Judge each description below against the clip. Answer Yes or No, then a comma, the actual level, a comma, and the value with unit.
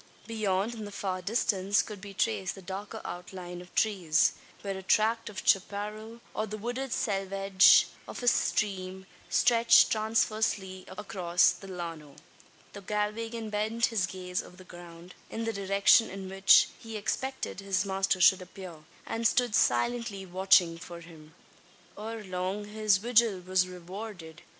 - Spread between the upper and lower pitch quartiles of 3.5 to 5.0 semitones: No, average, 2.8 semitones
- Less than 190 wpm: Yes, average, 150 wpm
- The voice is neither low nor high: No, high, 195 Hz